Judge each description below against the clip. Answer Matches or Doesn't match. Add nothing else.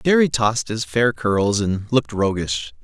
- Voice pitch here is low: Matches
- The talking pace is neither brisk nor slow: Matches